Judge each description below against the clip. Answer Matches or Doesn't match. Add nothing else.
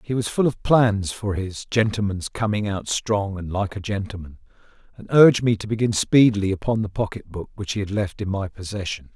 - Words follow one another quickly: Matches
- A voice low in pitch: Matches